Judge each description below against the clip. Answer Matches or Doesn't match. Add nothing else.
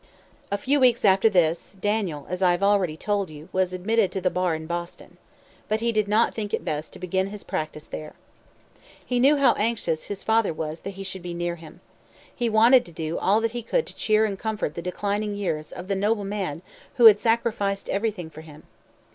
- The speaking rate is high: Matches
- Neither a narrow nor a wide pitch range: Matches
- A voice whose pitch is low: Doesn't match